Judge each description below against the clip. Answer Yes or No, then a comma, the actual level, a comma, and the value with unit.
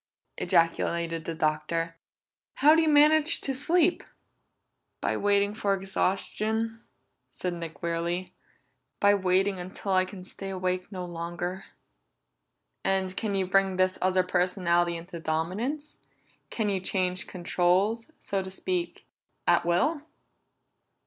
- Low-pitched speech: No, medium, 185 Hz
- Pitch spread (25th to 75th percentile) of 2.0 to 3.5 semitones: Yes, average, 2.8 semitones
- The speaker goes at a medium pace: No, slow, 120 wpm